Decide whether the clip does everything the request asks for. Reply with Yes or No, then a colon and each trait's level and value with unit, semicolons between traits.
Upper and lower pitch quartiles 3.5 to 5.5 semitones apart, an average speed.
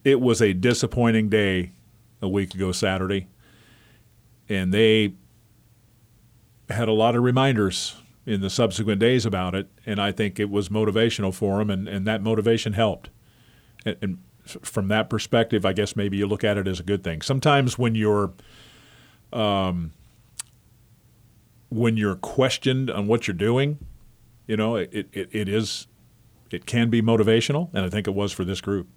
No: narrow, 2.6 semitones; average, 165 wpm